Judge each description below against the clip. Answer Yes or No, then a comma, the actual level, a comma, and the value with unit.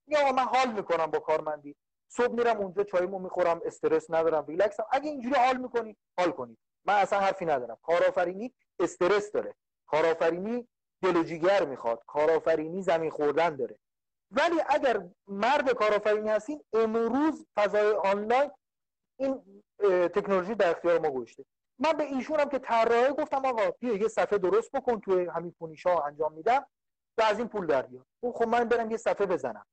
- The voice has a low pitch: No, high, 215 Hz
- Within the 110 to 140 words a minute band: No, fast, 155 wpm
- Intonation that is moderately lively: No, wide, 7.0 semitones